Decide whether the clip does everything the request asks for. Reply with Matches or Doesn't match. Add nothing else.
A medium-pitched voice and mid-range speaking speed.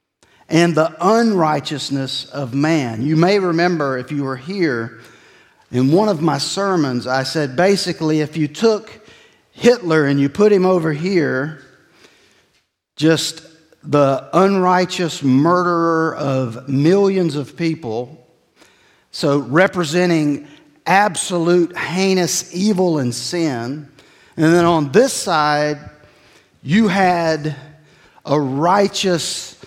Doesn't match